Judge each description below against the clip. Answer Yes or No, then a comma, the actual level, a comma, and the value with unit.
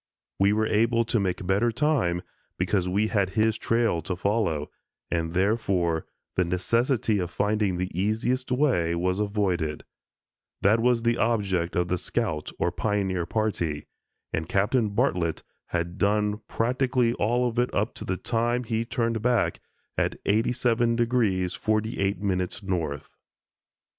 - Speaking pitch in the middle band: No, low, 105 Hz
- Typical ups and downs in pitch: Yes, average, 4.2 semitones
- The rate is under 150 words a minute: Yes, average, 140 wpm